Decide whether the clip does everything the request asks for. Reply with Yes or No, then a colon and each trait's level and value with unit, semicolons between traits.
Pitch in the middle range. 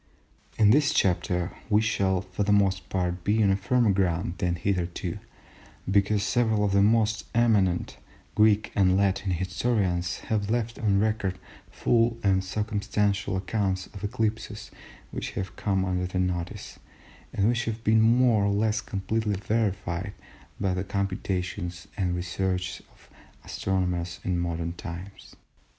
No: low, 100 Hz